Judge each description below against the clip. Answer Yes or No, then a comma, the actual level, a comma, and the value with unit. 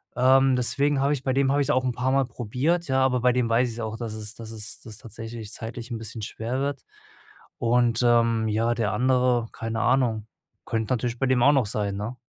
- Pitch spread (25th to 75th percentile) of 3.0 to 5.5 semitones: No, narrow, 2.5 semitones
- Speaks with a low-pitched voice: Yes, low, 120 Hz